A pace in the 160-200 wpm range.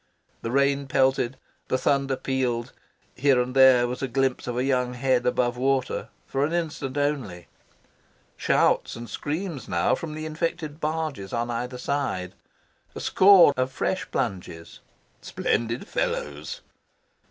No: average, 140 wpm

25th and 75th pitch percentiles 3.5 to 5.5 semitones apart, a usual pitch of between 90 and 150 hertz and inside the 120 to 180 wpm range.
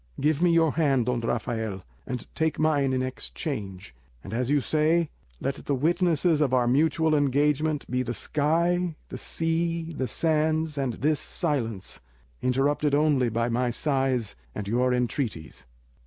Yes: average, 4.1 semitones; medium, 140 Hz; average, 150 wpm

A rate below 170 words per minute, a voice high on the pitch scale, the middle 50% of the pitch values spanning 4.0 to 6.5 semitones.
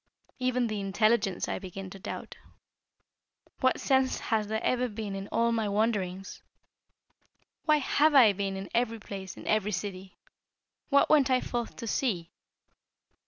Yes: average, 150 wpm; high, 215 Hz; average, 4.3 semitones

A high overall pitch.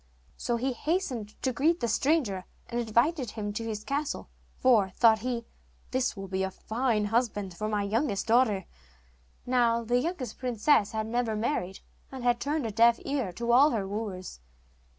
Yes: high, 235 Hz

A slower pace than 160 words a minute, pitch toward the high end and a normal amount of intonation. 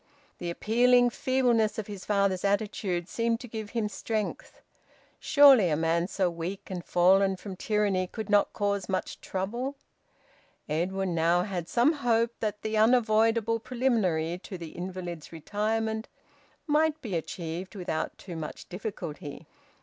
Yes: average, 140 wpm; high, 200 Hz; average, 4.2 semitones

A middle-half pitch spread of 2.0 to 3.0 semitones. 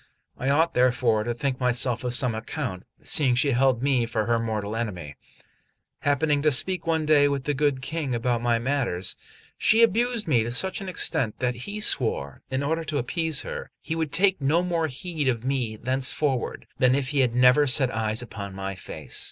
No: average, 4.4 semitones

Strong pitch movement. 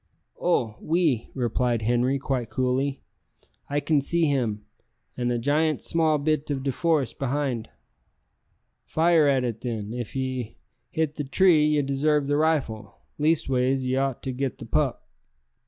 No: average, 3.5 semitones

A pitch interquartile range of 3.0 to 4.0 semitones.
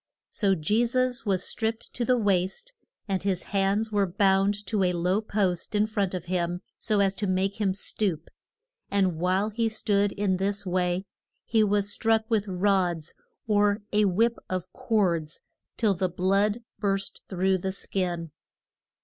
No: narrow, 2.4 semitones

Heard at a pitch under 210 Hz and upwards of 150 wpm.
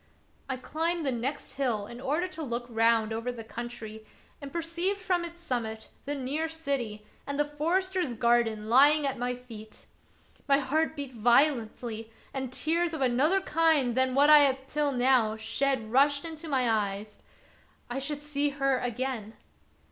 No: very high, 265 Hz; average, 165 wpm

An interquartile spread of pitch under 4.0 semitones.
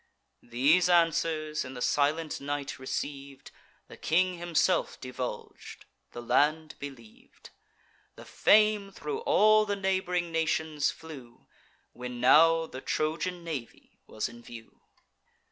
No: average, 4.8 semitones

